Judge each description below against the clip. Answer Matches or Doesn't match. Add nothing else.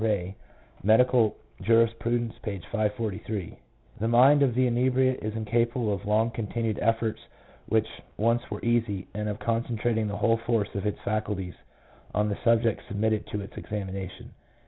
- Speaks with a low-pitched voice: Matches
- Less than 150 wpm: Doesn't match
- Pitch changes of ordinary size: Doesn't match